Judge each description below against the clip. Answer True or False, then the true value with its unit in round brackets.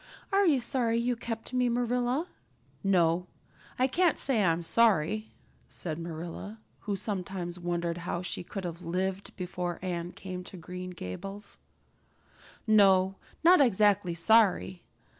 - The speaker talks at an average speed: False (130 wpm)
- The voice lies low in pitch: False (190 Hz)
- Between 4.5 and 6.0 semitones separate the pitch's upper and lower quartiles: True (4.8 semitones)